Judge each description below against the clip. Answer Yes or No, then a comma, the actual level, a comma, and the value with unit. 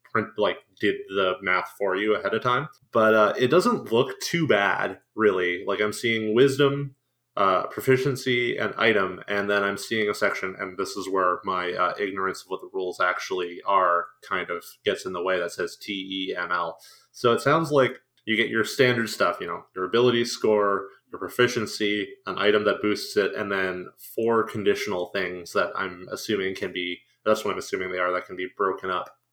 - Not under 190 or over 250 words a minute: Yes, average, 200 wpm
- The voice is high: No, low, 105 Hz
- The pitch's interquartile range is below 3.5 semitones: No, average, 4.6 semitones